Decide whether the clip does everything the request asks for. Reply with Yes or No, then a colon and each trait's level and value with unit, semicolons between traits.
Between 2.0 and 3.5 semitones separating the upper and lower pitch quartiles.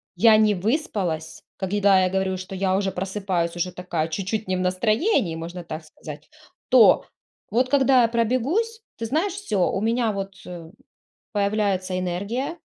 No: average, 4.2 semitones